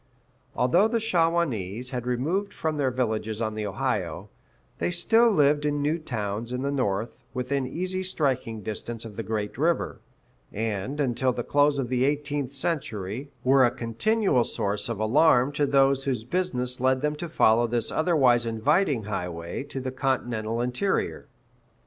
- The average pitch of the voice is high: No, low, 130 Hz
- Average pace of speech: Yes, average, 160 wpm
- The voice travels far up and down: No, average, 4.5 semitones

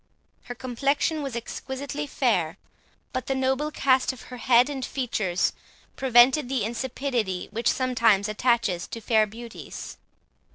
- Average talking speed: No, slow, 130 wpm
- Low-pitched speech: No, high, 245 Hz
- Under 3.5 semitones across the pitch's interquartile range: Yes, average, 2.9 semitones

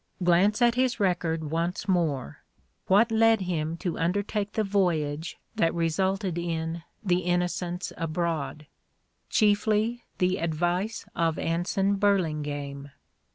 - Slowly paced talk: Yes, slow, 110 wpm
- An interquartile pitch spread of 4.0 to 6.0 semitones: No, average, 3.6 semitones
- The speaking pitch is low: No, medium, 175 Hz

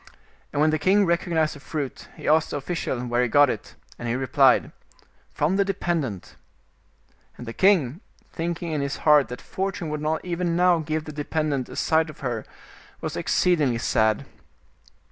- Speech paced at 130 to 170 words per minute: No, average, 180 wpm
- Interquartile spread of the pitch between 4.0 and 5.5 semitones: Yes, average, 4.3 semitones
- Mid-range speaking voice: Yes, medium, 155 Hz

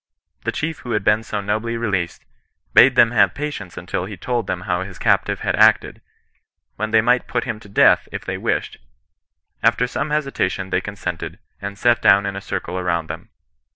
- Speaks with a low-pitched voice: Yes, low, 105 Hz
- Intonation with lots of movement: No, average, 3.9 semitones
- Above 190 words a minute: Yes, average, 200 wpm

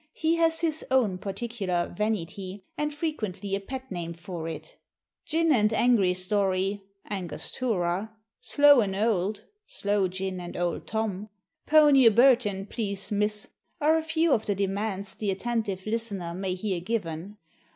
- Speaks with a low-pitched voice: No, high, 205 Hz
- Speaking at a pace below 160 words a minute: Yes, average, 145 wpm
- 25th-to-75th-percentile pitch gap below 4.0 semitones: No, average, 4.3 semitones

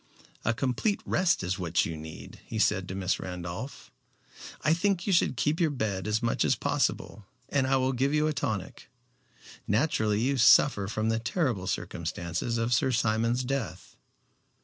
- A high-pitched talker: No, low, 115 Hz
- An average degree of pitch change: No, wide, 6.0 semitones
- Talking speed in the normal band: Yes, average, 170 wpm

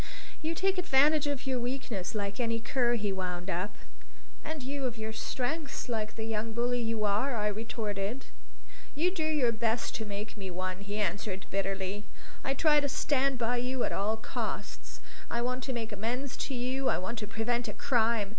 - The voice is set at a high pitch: Yes, high, 230 Hz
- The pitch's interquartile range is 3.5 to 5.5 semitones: Yes, average, 4.2 semitones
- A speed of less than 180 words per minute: No, average, 190 wpm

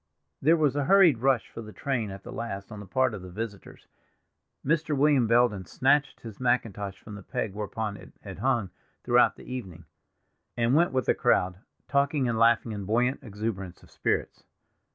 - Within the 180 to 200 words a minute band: Yes, average, 185 wpm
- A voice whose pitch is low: Yes, low, 115 Hz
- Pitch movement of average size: Yes, average, 4.6 semitones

